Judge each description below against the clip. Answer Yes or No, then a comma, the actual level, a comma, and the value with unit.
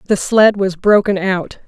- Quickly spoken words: No, average, 180 wpm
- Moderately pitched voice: No, high, 195 Hz